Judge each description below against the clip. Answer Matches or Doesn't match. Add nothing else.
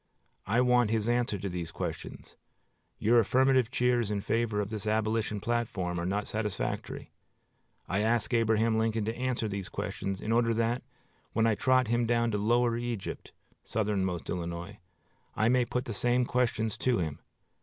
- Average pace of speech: Matches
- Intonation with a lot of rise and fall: Doesn't match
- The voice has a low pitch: Matches